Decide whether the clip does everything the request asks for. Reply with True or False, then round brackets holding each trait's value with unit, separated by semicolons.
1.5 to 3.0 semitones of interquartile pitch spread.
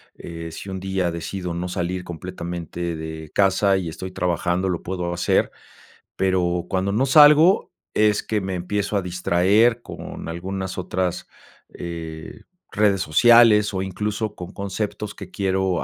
True (2.4 semitones)